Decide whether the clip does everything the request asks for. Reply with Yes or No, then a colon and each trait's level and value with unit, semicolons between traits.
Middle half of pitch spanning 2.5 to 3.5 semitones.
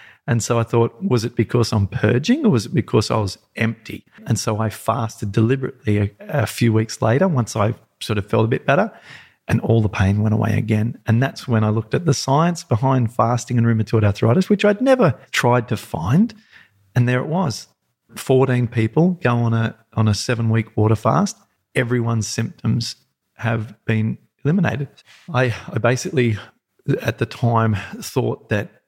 Yes: average, 2.9 semitones